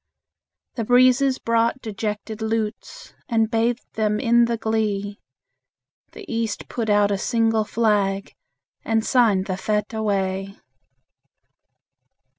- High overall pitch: Yes, high, 220 Hz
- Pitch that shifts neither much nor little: No, narrow, 2.0 semitones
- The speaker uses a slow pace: Yes, slow, 110 wpm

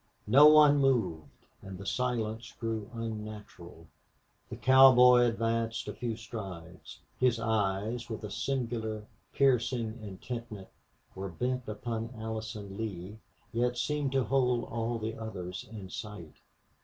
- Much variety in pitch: No, average, 2.7 semitones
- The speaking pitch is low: Yes, low, 115 Hz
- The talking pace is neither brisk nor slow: No, slow, 125 wpm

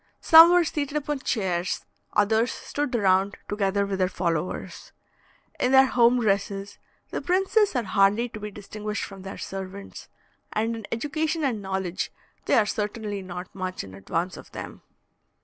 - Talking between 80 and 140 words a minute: No, average, 155 wpm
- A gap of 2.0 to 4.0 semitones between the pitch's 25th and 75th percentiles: No, average, 4.6 semitones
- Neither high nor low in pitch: No, high, 210 Hz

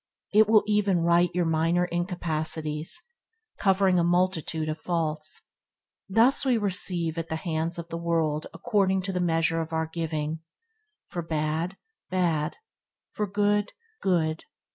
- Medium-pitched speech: Yes, medium, 170 Hz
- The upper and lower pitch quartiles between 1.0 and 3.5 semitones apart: Yes, average, 2.9 semitones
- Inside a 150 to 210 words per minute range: No, average, 140 wpm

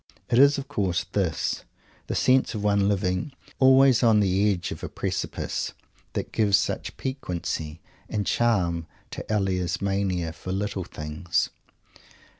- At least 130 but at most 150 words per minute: Yes, average, 140 wpm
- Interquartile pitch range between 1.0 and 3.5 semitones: No, average, 3.9 semitones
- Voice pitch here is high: No, low, 100 Hz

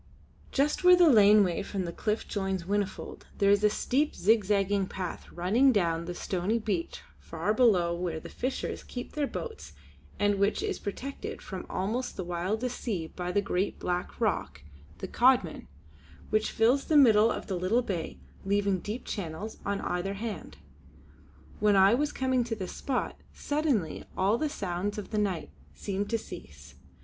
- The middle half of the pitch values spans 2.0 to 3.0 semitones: No, average, 4.0 semitones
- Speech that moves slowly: No, average, 170 wpm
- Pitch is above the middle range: Yes, high, 205 Hz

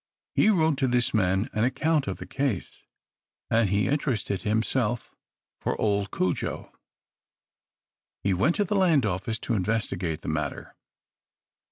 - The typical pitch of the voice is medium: No, low, 110 Hz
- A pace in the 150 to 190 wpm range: No, average, 140 wpm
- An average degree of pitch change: No, wide, 6.0 semitones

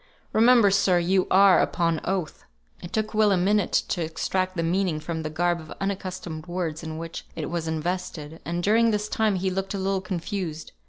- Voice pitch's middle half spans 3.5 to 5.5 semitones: No, average, 2.9 semitones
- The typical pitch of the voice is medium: Yes, medium, 180 Hz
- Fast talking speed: No, average, 195 wpm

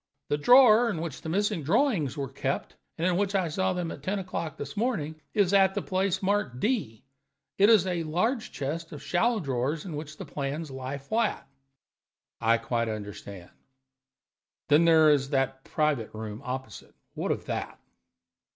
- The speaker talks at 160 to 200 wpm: Yes, average, 170 wpm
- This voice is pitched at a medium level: Yes, medium, 160 Hz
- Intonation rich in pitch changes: Yes, wide, 6.1 semitones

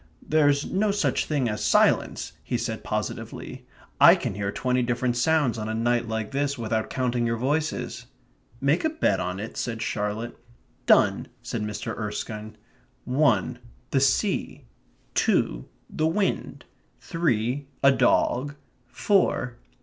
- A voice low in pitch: Yes, low, 125 Hz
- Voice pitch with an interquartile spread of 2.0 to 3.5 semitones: No, average, 4.5 semitones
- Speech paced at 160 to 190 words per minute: No, slow, 135 wpm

